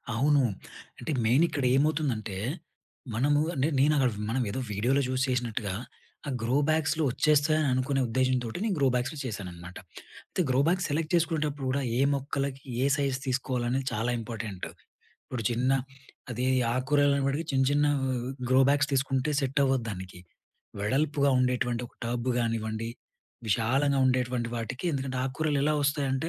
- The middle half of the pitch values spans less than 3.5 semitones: Yes, average, 2.9 semitones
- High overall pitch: No, low, 130 Hz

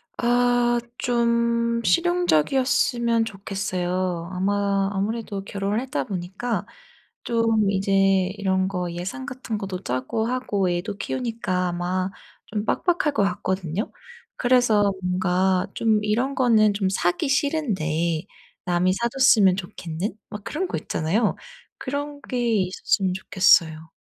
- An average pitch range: Yes, average, 4.5 semitones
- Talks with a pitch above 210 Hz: No, high, 200 Hz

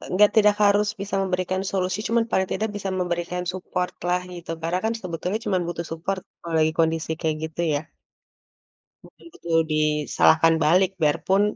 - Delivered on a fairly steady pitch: No, average, 3.0 semitones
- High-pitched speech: No, medium, 180 Hz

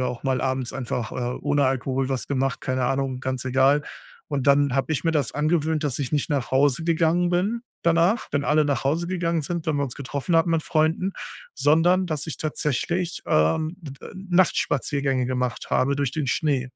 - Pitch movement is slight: No, average, 3.7 semitones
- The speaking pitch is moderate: Yes, medium, 145 Hz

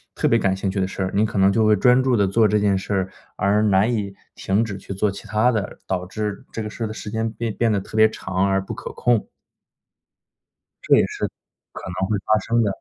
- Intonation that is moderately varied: No, narrow, 2.2 semitones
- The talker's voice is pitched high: No, low, 105 Hz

